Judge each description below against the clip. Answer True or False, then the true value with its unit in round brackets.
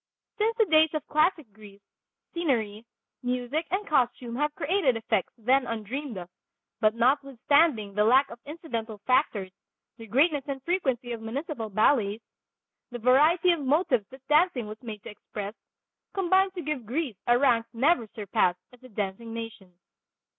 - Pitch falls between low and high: False (250 Hz)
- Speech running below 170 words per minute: True (155 wpm)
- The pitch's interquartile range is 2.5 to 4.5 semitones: False (5.4 semitones)